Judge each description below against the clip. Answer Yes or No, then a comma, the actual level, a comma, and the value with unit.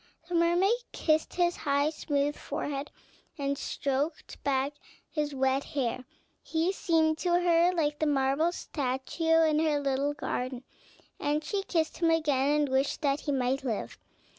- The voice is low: No, very high, 295 Hz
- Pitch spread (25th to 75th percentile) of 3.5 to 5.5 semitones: No, average, 3.0 semitones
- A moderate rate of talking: Yes, average, 150 wpm